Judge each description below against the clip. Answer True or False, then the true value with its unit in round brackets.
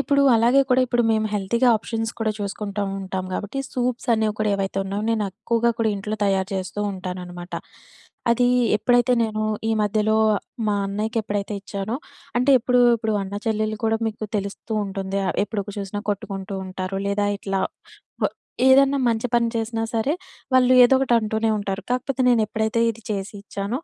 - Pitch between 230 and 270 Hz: False (215 Hz)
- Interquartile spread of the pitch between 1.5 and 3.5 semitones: True (2.9 semitones)